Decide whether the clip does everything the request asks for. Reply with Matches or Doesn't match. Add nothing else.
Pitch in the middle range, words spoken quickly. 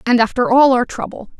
Doesn't match